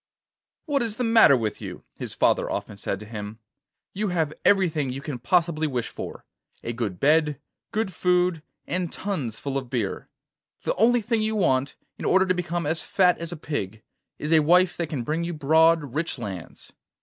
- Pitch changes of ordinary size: No, wide, 5.7 semitones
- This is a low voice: No, medium, 160 Hz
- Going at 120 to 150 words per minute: No, average, 190 wpm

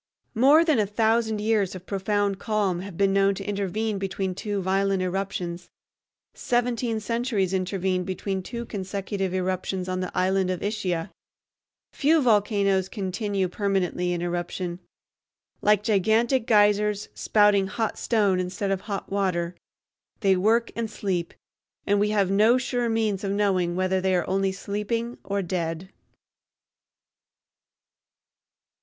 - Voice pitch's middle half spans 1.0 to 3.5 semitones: Yes, narrow, 2.4 semitones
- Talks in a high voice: Yes, high, 195 Hz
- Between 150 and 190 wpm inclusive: No, slow, 135 wpm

